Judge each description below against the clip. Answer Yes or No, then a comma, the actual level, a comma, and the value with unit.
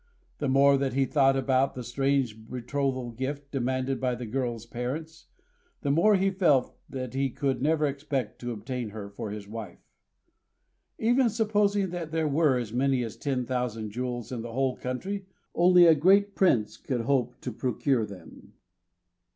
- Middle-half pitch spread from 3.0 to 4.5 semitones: Yes, average, 3.7 semitones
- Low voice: Yes, low, 130 Hz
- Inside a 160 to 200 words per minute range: Yes, average, 165 wpm